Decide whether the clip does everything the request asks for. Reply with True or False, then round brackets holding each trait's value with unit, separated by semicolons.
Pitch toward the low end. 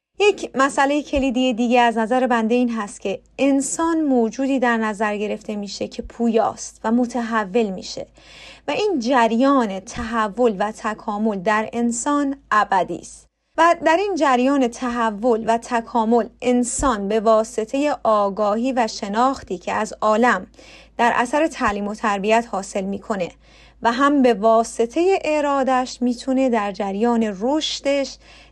False (235 Hz)